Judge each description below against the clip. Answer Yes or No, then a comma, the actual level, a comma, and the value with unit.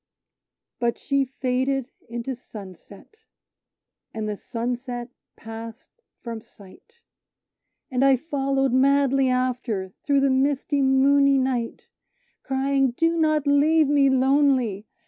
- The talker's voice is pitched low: No, very high, 265 Hz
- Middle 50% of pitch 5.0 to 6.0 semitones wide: No, narrow, 2.6 semitones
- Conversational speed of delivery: No, slow, 105 wpm